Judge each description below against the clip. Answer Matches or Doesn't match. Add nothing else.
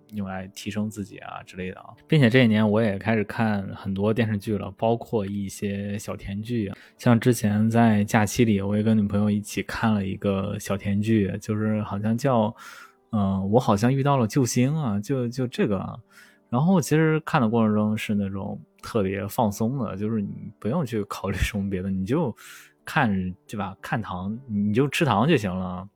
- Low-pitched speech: Matches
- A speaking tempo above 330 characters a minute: Doesn't match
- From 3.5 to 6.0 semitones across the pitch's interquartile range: Doesn't match